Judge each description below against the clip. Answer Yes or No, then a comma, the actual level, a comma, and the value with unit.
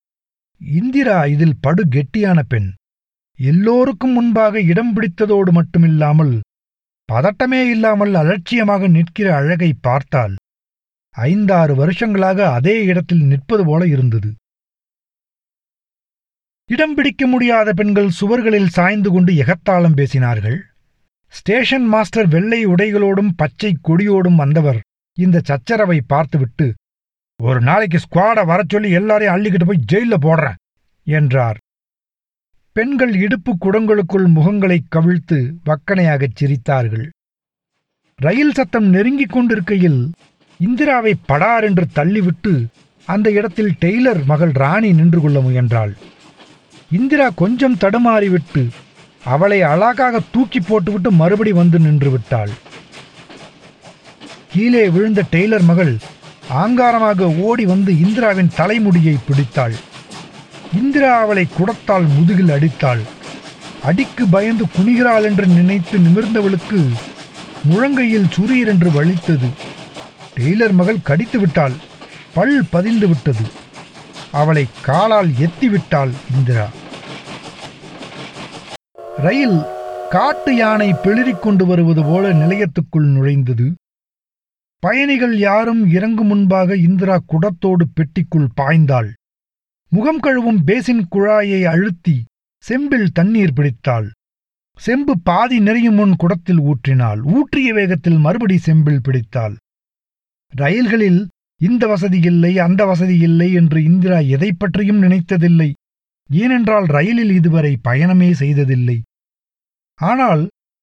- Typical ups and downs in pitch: No, wide, 5.8 semitones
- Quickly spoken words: No, average, 95 wpm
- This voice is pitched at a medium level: Yes, medium, 180 Hz